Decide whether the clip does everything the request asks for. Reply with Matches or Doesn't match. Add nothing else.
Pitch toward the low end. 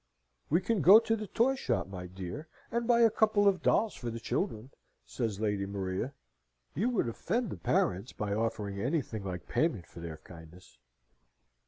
Matches